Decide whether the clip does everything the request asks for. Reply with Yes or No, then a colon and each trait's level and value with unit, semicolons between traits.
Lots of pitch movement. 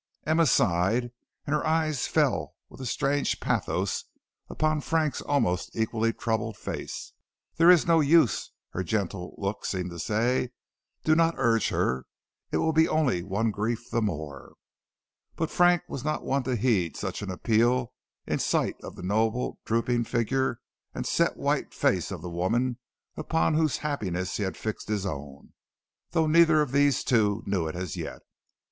Yes: wide, 7.0 semitones